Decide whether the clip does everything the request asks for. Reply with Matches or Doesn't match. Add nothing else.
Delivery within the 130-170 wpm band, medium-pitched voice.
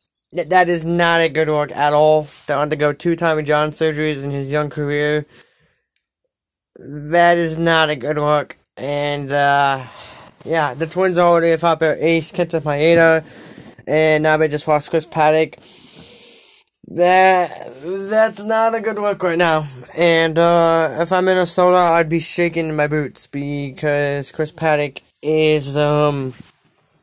Matches